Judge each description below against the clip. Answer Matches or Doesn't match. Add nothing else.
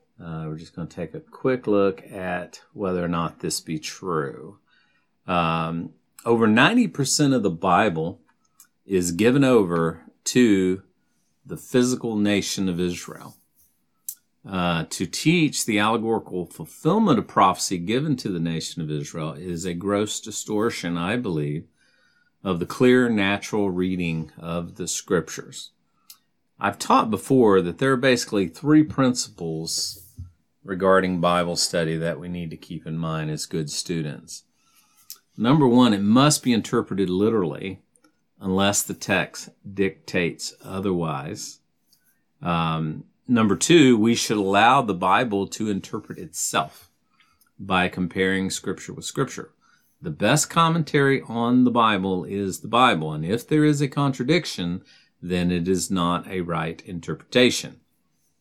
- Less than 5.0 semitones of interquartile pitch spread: Doesn't match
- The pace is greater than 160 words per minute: Doesn't match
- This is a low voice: Matches